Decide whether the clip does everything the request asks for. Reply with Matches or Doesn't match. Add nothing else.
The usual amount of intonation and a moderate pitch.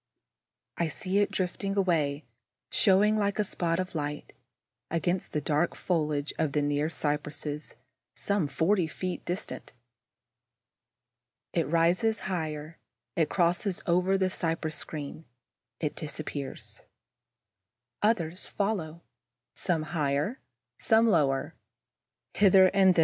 Matches